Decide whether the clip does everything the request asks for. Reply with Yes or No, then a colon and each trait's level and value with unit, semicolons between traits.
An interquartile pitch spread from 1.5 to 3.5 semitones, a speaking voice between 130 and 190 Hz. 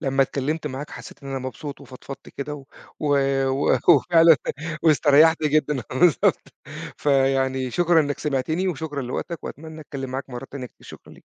Yes: average, 2.8 semitones; medium, 140 Hz